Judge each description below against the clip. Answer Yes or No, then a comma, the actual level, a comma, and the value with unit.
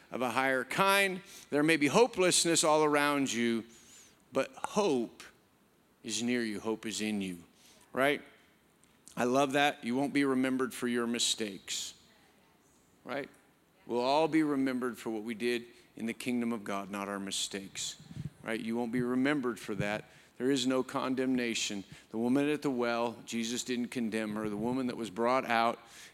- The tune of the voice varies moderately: Yes, average, 3.5 semitones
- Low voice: Yes, low, 120 Hz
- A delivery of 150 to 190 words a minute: Yes, average, 170 wpm